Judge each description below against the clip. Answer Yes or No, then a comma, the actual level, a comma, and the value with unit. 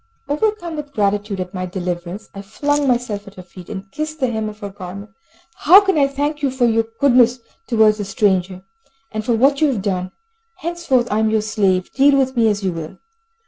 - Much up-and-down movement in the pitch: Yes, wide, 5.9 semitones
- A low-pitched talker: No, high, 220 Hz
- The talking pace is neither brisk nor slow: No, fast, 210 wpm